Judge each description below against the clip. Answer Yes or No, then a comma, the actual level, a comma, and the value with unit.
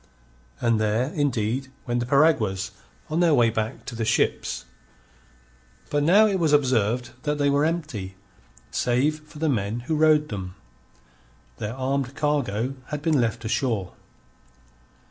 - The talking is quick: No, average, 145 wpm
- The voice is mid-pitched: No, low, 130 Hz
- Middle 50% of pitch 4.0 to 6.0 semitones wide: Yes, average, 4.9 semitones